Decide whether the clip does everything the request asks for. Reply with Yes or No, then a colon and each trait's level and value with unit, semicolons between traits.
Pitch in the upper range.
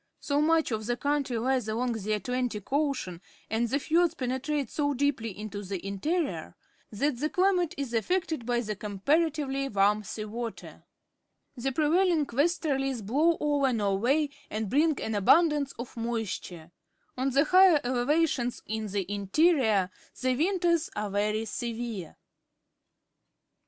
Yes: very high, 255 Hz